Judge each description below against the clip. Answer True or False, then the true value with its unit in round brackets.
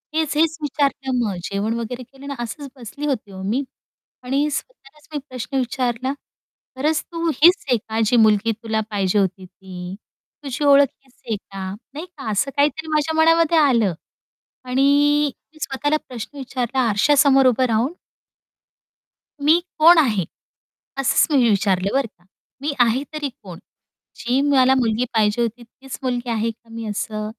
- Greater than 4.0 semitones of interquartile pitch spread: True (4.6 semitones)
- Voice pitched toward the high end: True (255 Hz)